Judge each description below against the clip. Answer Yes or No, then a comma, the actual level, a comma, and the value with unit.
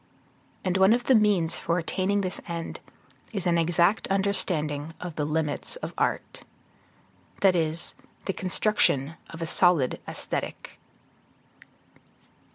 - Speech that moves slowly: Yes, slow, 125 wpm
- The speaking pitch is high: No, medium, 175 Hz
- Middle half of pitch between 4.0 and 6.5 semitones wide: No, average, 3.2 semitones